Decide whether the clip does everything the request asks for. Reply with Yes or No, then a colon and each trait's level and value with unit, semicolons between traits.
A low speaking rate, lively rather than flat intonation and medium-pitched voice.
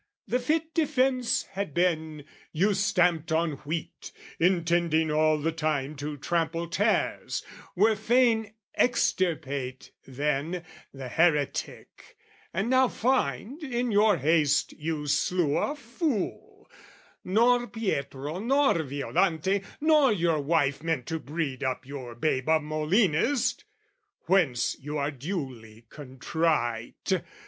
Yes: slow, 115 wpm; wide, 6.8 semitones; medium, 165 Hz